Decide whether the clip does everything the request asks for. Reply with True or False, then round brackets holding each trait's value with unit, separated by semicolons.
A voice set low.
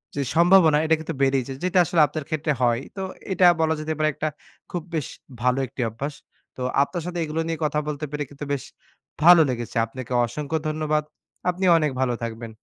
False (150 Hz)